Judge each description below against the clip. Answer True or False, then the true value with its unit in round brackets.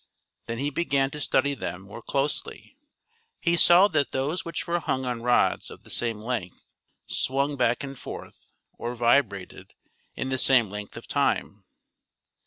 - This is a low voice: True (130 Hz)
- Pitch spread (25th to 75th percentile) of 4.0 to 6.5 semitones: False (3.4 semitones)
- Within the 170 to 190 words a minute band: False (160 wpm)